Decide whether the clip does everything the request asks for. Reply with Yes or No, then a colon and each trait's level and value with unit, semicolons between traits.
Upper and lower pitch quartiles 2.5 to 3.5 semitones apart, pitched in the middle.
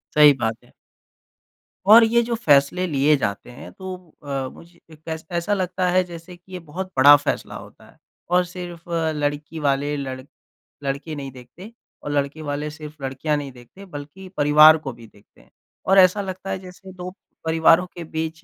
No: average, 4.3 semitones; medium, 155 Hz